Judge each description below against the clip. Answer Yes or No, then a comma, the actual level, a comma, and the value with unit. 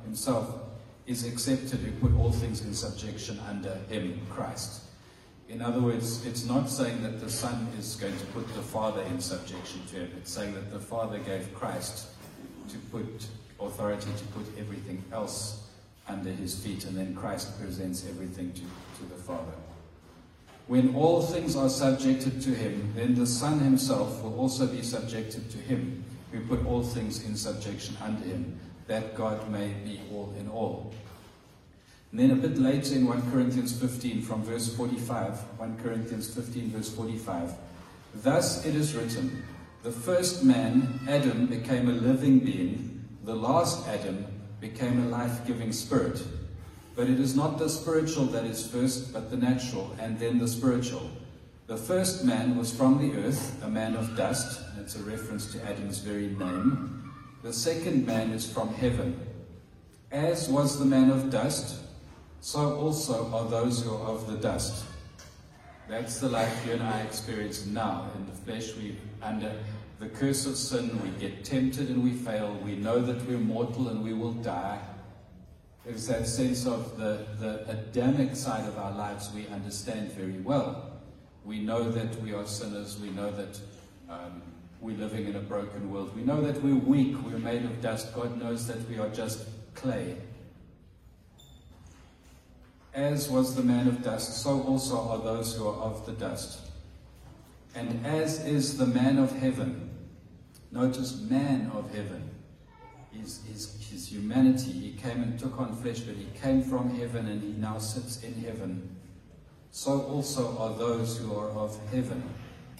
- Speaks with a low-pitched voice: Yes, low, 115 Hz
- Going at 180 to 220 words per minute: No, average, 165 wpm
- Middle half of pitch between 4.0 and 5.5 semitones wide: No, average, 3.6 semitones